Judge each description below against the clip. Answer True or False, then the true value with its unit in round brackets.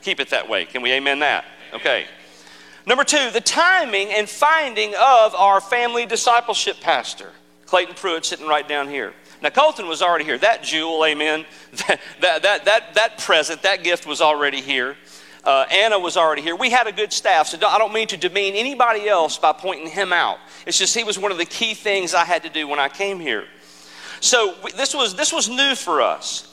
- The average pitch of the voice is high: True (195 Hz)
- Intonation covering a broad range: True (7.1 semitones)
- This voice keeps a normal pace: False (210 wpm)